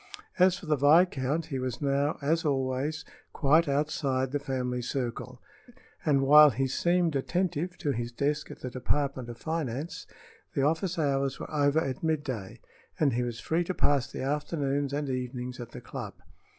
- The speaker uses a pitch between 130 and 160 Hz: Yes, medium, 140 Hz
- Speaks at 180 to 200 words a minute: No, average, 170 wpm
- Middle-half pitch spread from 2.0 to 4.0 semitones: Yes, average, 3.0 semitones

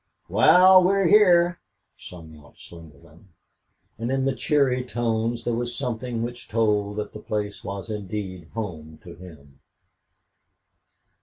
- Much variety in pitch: Yes, wide, 5.9 semitones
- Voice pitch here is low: Yes, low, 110 Hz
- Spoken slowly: Yes, slow, 130 wpm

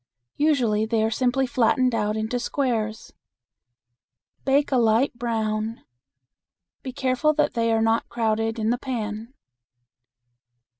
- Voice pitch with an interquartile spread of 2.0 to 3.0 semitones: Yes, average, 2.7 semitones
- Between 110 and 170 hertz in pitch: No, high, 230 Hz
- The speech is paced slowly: Yes, slow, 120 wpm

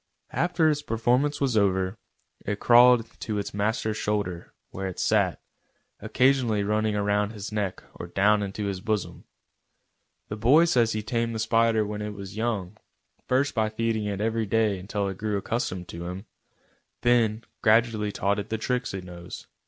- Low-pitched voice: Yes, low, 105 Hz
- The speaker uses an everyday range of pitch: No, narrow, 2.3 semitones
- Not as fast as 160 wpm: No, average, 170 wpm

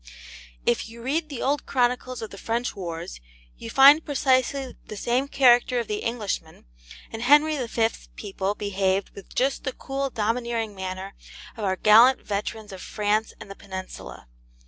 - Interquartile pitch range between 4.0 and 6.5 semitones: Yes, average, 4.5 semitones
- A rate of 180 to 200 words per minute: No, average, 160 wpm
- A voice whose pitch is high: Yes, high, 230 Hz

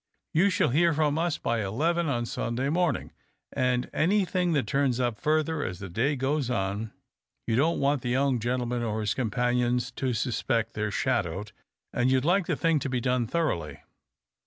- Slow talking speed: No, average, 185 wpm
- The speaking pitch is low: Yes, low, 125 Hz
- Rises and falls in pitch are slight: No, average, 4.7 semitones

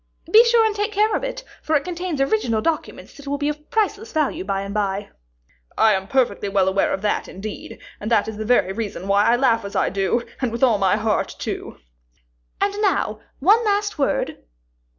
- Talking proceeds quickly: Yes, fast, 210 wpm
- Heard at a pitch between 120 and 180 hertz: No, high, 240 Hz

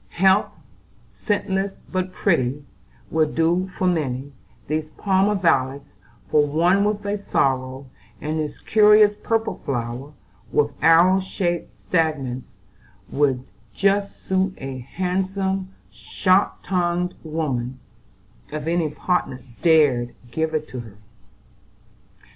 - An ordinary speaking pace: No, slow, 110 wpm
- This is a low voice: No, medium, 165 Hz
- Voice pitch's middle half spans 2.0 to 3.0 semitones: No, average, 5.3 semitones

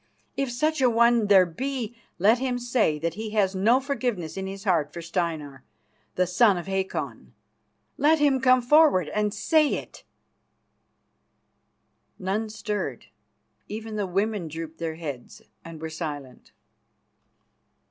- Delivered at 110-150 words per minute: Yes, slow, 135 wpm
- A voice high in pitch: Yes, high, 205 Hz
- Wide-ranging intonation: Yes, wide, 6.4 semitones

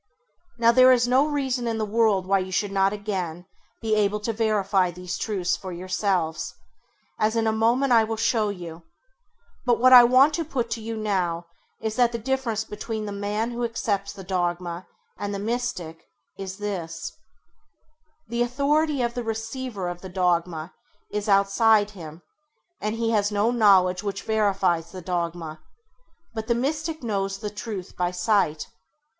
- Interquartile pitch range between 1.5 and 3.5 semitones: No, average, 3.9 semitones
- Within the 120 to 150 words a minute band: No, average, 170 wpm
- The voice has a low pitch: No, high, 210 Hz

